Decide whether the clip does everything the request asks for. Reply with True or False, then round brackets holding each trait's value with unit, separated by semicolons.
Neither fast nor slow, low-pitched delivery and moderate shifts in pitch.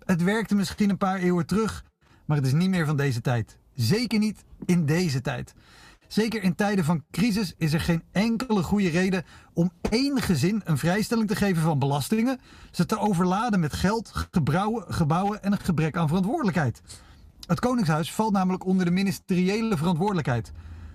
False (170 wpm; 185 Hz; 4.3 semitones)